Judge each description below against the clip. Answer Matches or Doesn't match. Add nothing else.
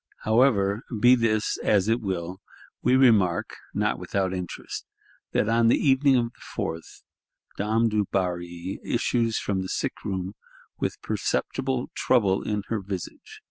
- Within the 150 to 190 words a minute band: Doesn't match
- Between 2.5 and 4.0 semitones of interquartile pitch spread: Matches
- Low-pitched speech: Matches